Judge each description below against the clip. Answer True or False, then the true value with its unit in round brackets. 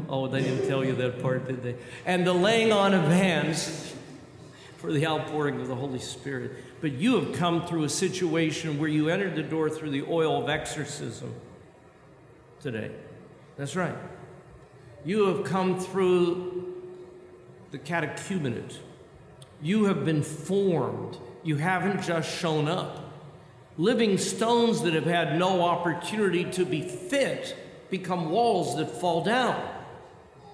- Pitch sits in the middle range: True (165 Hz)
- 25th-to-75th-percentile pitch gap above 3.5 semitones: True (3.9 semitones)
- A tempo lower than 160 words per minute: True (140 wpm)